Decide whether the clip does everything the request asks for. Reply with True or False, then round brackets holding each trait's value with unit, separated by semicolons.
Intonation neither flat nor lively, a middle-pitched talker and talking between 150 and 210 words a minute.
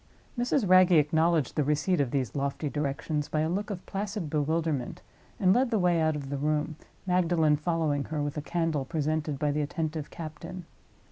True (3.0 semitones; 155 Hz; 185 wpm)